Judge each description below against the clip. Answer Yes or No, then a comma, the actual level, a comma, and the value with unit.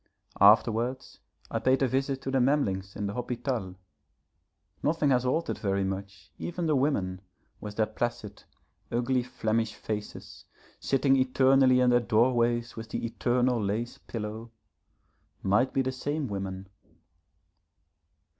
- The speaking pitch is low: Yes, low, 120 Hz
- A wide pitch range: No, average, 3.8 semitones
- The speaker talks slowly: Yes, slow, 130 wpm